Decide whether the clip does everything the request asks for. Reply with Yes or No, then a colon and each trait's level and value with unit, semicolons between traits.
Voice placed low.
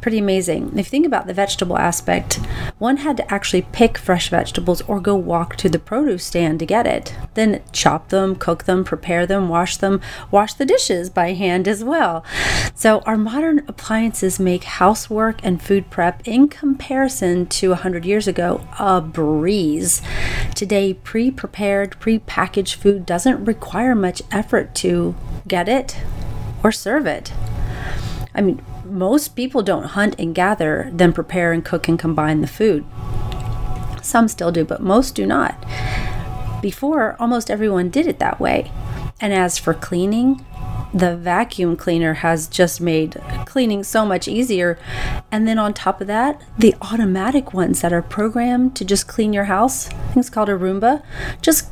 No: high, 190 Hz